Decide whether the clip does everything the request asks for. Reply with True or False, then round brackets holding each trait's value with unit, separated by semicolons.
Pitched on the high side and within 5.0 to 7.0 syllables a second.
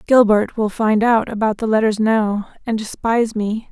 False (220 Hz; 4.7 syllables/s)